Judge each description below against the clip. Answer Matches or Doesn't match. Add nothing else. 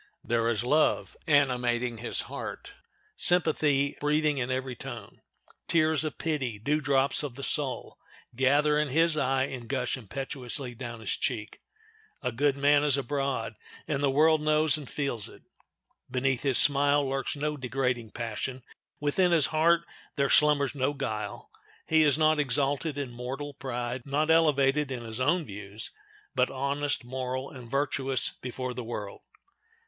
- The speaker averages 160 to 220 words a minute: Doesn't match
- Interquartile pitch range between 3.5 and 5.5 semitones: Doesn't match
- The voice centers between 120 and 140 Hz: Matches